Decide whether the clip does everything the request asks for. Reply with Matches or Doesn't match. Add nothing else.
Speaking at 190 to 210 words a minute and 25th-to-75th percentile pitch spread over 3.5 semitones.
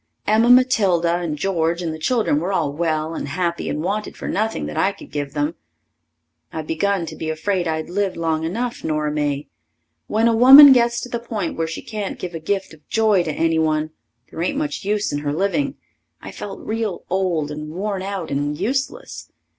Matches